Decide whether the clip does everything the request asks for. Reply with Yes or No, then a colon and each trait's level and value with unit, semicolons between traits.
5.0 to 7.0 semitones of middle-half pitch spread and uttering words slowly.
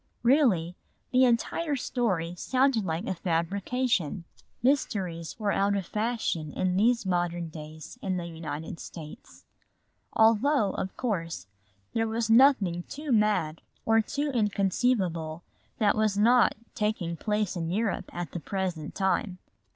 Yes: wide, 5.4 semitones; slow, 130 wpm